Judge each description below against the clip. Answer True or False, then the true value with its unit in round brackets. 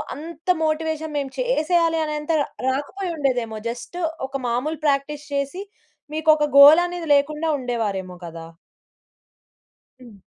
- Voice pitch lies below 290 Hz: False (295 Hz)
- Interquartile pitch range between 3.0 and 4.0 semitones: True (3.7 semitones)